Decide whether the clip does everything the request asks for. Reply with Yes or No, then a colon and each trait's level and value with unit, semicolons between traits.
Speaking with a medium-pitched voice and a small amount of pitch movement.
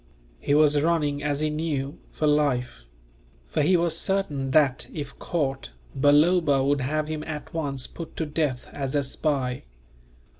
Yes: medium, 145 Hz; narrow, 2.2 semitones